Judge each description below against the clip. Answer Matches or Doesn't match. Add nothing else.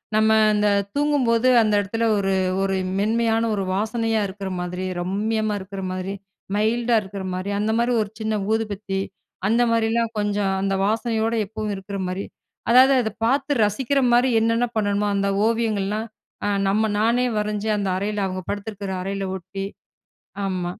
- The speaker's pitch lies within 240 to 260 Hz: Doesn't match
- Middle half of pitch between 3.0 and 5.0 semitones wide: Doesn't match